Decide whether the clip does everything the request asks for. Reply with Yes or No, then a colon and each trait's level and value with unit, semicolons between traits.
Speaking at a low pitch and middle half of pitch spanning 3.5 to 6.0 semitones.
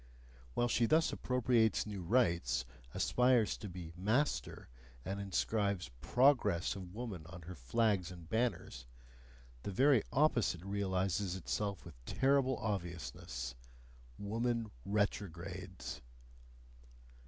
Yes: low, 100 Hz; average, 5.1 semitones